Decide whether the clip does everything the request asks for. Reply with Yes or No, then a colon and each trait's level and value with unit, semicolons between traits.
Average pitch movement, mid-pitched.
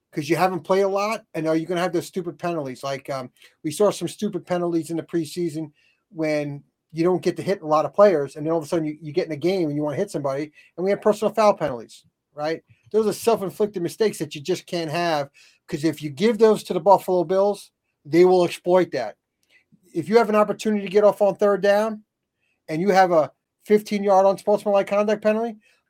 Yes: average, 4.2 semitones; medium, 180 Hz